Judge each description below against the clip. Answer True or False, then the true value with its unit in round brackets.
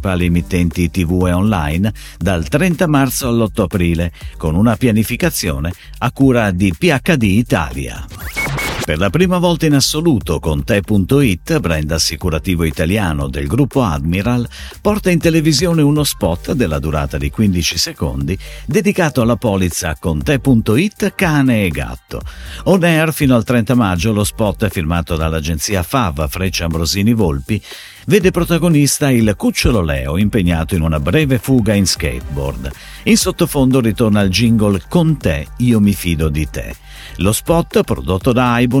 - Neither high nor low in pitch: False (105 Hz)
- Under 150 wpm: True (140 wpm)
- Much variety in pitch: True (8.2 semitones)